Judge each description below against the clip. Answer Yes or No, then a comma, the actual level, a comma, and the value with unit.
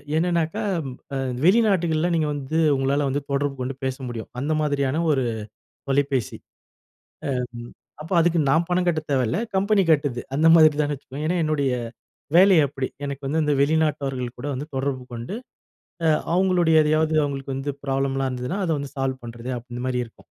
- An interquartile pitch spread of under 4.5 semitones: Yes, average, 3.3 semitones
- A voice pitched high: No, medium, 145 Hz